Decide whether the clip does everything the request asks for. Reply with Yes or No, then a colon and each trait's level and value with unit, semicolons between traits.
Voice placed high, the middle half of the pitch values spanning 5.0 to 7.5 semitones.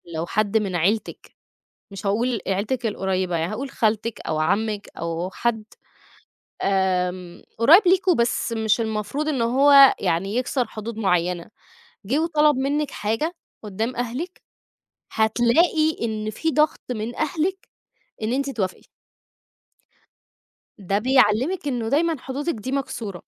Yes: high, 225 Hz; wide, 5.6 semitones